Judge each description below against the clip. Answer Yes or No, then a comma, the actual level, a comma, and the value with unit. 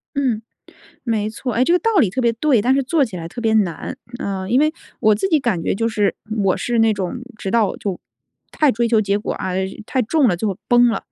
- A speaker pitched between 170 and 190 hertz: No, high, 225 Hz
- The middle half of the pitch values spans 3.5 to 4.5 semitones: Yes, average, 4.1 semitones